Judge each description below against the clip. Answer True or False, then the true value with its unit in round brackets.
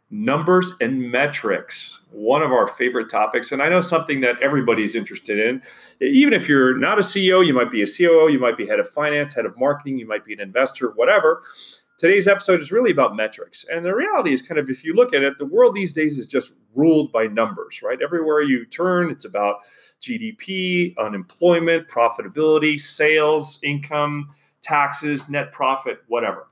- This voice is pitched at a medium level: True (155 Hz)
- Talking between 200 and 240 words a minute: False (190 wpm)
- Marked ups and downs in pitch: True (5.9 semitones)